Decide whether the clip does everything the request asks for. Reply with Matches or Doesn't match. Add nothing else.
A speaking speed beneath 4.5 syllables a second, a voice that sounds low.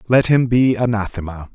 Doesn't match